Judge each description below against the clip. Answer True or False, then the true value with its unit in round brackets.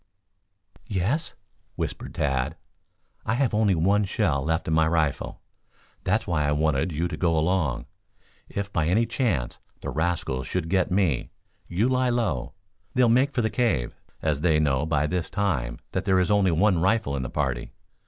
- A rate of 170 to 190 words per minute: True (175 wpm)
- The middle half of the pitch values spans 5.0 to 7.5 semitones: True (5.3 semitones)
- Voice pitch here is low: True (85 Hz)